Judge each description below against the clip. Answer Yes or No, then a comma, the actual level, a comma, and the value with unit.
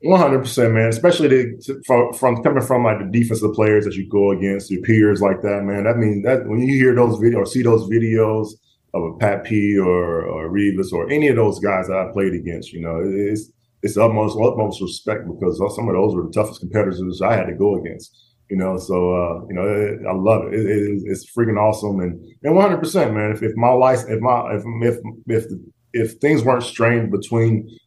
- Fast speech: Yes, fast, 235 wpm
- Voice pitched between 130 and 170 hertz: No, low, 110 Hz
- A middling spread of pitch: Yes, average, 3.2 semitones